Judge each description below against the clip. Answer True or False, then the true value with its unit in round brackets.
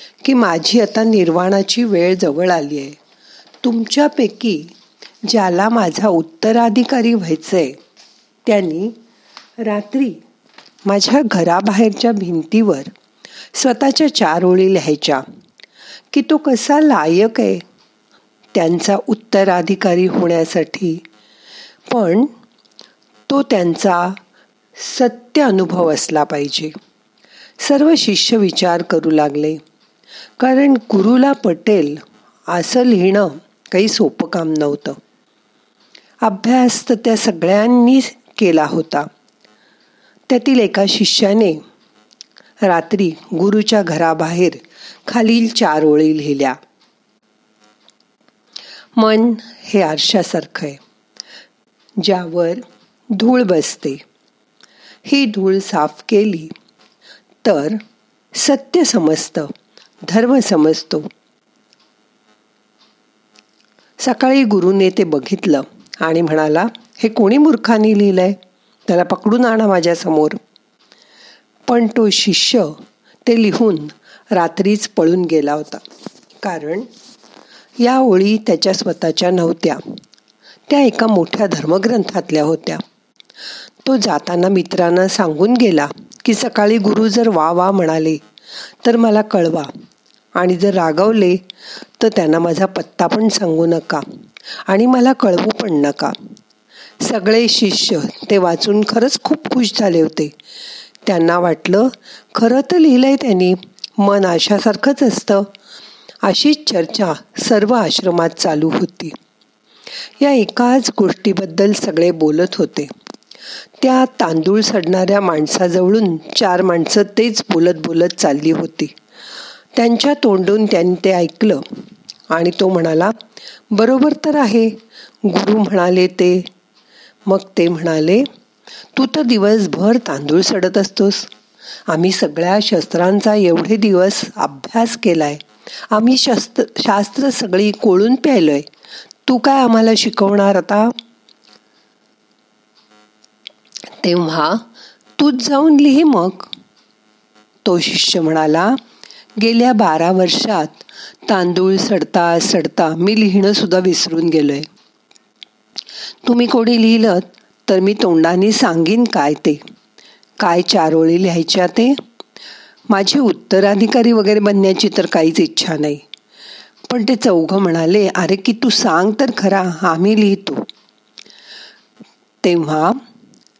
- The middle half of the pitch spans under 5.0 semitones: False (5.4 semitones)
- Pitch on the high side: True (195 Hz)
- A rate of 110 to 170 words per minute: False (95 wpm)